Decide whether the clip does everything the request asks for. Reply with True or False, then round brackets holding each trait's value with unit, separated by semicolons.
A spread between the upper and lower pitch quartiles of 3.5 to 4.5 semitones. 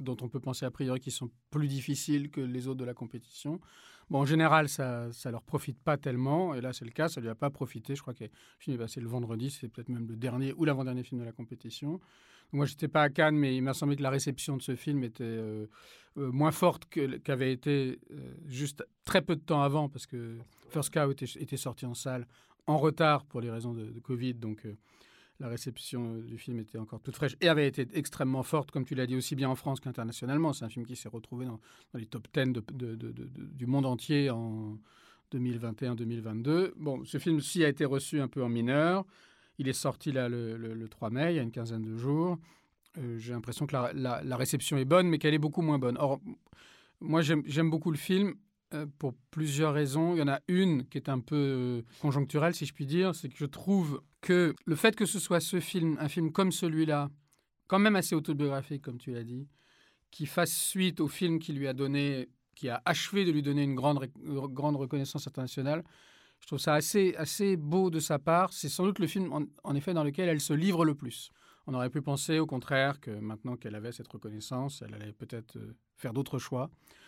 True (3.8 semitones)